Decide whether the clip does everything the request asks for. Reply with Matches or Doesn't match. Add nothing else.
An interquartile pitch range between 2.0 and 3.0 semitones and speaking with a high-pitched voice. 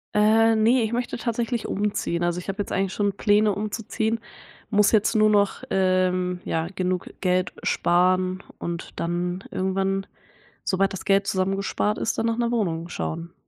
Matches